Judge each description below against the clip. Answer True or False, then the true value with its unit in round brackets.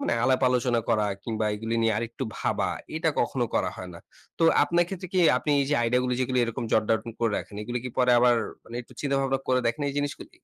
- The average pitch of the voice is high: False (125 Hz)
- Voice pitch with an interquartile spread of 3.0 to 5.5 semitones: False (2.6 semitones)